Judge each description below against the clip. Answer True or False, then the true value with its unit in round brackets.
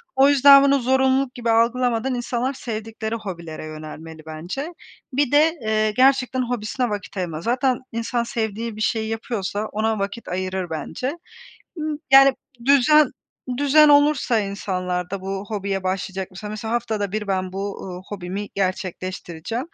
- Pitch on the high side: True (220 Hz)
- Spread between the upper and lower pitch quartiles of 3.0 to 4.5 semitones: False (5.2 semitones)